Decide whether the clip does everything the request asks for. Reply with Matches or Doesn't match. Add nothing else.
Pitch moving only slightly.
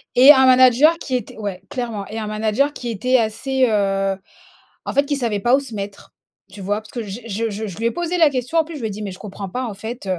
Doesn't match